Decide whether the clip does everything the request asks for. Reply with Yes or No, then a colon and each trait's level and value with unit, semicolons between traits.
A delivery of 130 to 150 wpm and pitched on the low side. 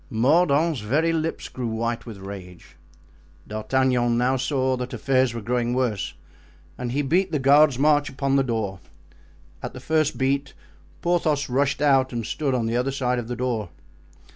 No: average, 165 wpm; low, 130 Hz